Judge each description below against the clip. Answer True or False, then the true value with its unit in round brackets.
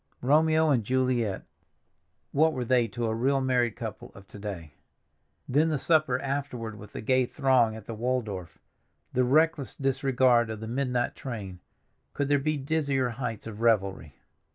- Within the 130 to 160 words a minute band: True (150 wpm)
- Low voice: True (125 Hz)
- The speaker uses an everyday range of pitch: True (3.7 semitones)